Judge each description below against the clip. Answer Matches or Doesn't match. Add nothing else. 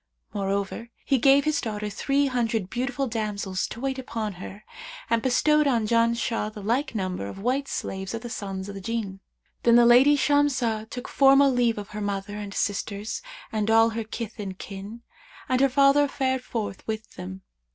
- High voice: Matches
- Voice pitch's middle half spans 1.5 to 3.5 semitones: Doesn't match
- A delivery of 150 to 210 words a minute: Matches